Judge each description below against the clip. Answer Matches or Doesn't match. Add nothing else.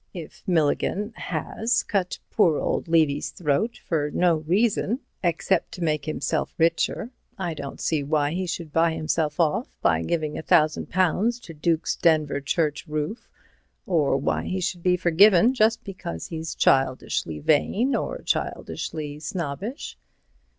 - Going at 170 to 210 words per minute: Doesn't match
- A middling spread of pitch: Matches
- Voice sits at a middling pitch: Matches